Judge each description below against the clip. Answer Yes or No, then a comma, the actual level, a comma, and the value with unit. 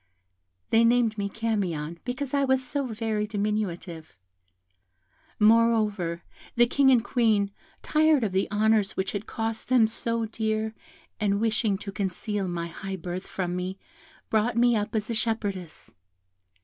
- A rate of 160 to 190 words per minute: No, average, 145 wpm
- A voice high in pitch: Yes, high, 215 Hz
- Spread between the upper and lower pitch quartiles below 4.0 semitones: Yes, average, 3.0 semitones